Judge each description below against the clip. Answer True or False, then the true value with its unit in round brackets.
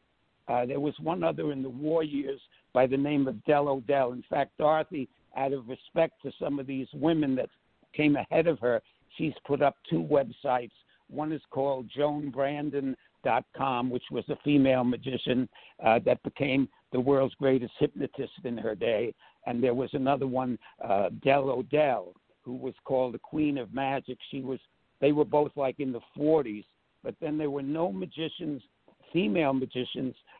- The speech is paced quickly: False (170 wpm)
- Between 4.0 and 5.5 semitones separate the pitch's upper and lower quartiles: False (2.4 semitones)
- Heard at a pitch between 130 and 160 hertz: True (140 Hz)